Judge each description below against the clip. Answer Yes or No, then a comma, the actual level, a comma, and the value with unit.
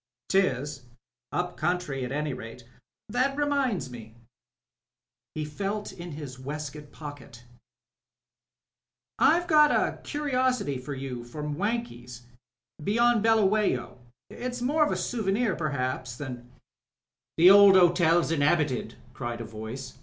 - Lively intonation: Yes, wide, 8.7 semitones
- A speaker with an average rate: No, slow, 130 wpm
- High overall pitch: No, medium, 155 Hz